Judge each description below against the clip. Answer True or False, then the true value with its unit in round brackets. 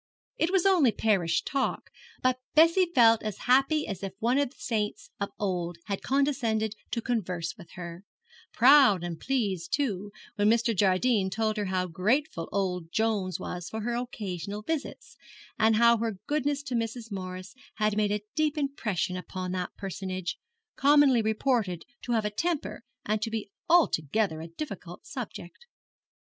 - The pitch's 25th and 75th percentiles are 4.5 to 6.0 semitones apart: True (5.5 semitones)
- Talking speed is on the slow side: False (160 wpm)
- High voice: True (215 Hz)